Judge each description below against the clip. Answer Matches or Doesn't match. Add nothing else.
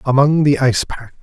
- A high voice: Doesn't match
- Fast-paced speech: Doesn't match